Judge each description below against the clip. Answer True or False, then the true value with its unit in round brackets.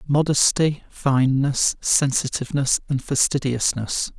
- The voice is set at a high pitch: False (135 Hz)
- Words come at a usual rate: False (70 wpm)